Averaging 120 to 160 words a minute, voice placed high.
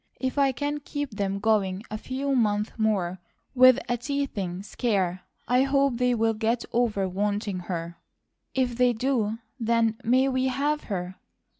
Yes: average, 155 wpm; high, 230 Hz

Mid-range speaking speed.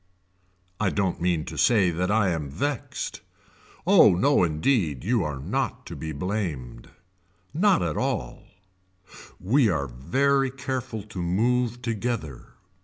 No: slow, 130 wpm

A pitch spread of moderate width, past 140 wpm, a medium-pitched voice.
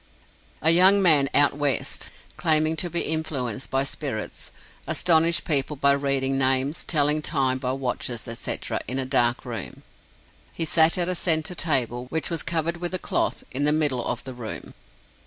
Yes: average, 3.7 semitones; average, 170 wpm; medium, 145 Hz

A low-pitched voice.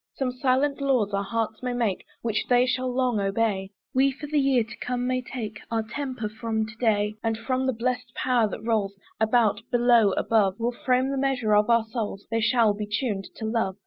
No: high, 230 Hz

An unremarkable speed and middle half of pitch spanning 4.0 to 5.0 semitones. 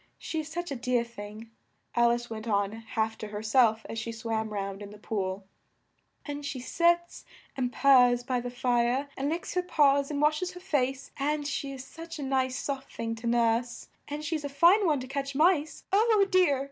No: fast, 210 wpm; average, 4.6 semitones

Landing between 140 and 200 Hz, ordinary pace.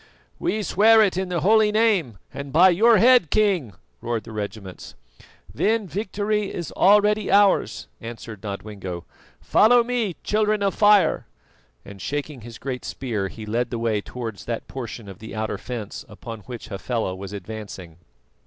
No: low, 130 Hz; average, 155 wpm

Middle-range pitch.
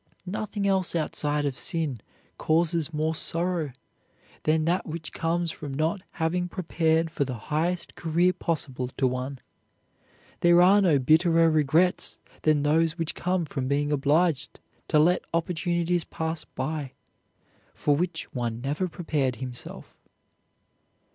Yes: medium, 160 Hz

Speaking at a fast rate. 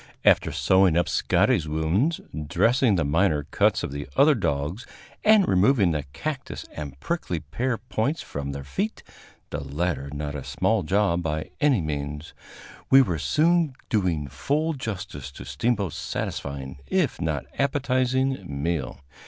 No: average, 145 wpm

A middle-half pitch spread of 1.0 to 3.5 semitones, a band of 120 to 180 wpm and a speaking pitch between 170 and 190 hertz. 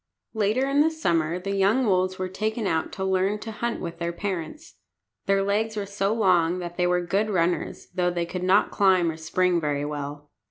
No: average, 3.2 semitones; fast, 205 wpm; medium, 185 Hz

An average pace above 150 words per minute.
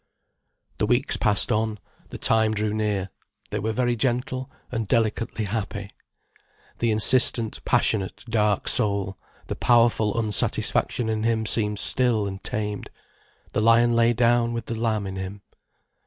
No: average, 140 wpm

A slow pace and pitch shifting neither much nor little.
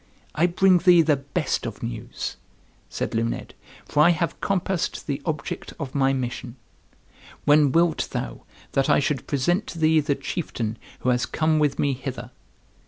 No: average, 165 wpm; average, 4.1 semitones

